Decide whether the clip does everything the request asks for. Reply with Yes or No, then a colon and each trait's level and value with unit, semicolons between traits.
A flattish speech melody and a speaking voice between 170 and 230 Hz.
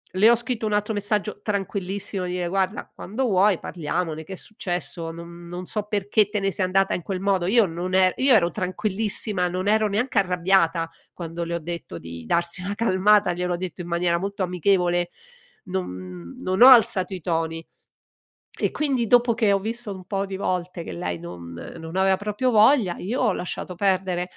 No: average, 3.2 semitones; medium, 185 Hz